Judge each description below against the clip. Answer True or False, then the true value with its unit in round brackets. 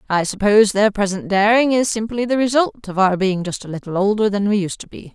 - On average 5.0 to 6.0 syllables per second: True (5.9 syllables/s)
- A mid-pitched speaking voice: False (205 Hz)